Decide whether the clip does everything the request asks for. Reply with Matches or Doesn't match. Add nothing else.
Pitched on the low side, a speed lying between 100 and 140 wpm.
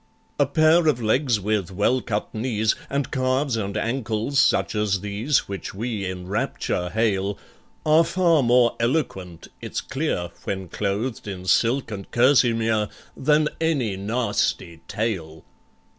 Matches